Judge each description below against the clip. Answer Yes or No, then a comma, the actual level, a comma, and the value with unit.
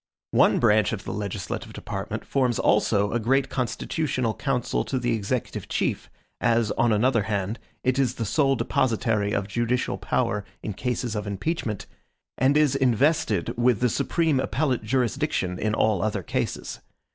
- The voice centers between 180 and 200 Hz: No, low, 120 Hz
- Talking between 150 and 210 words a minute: Yes, average, 155 wpm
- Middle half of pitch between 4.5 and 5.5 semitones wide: No, average, 3.8 semitones